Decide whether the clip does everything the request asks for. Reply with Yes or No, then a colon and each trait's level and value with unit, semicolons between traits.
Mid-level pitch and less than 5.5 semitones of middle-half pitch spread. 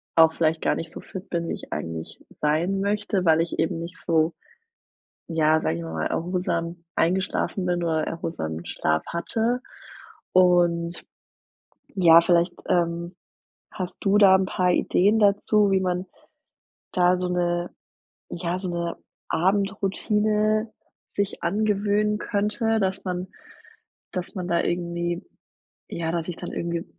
Yes: medium, 175 Hz; narrow, 2.5 semitones